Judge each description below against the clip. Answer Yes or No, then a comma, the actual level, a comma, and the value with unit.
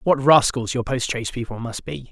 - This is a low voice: Yes, low, 125 Hz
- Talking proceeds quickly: Yes, fast, 225 wpm